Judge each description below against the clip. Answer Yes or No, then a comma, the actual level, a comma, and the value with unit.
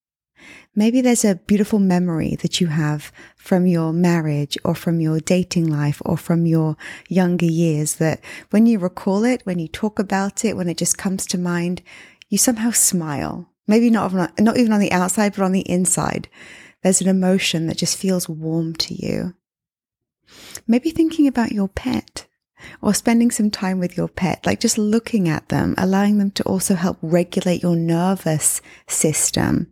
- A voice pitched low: No, medium, 185 Hz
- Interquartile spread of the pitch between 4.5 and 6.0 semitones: No, average, 3.8 semitones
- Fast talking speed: No, average, 175 wpm